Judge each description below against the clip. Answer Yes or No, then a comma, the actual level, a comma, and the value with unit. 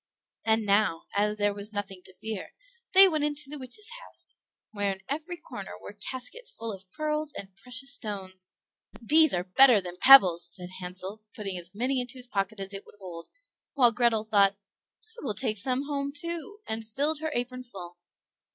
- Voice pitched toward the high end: Yes, high, 220 Hz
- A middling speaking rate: Yes, average, 185 wpm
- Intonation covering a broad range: Yes, wide, 5.9 semitones